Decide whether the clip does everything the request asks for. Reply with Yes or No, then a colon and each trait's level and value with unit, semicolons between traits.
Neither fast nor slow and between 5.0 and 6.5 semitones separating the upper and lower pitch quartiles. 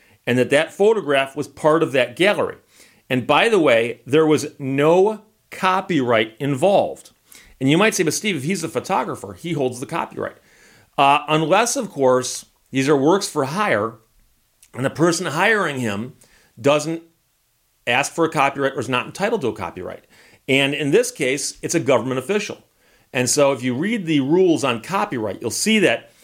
Yes: average, 180 wpm; wide, 5.6 semitones